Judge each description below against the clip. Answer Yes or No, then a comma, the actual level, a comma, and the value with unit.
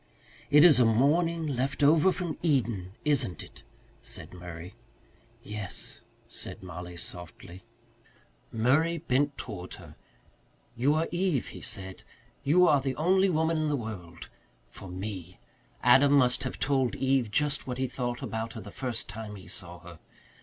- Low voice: Yes, low, 125 Hz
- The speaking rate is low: No, average, 155 wpm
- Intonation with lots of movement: Yes, wide, 7.2 semitones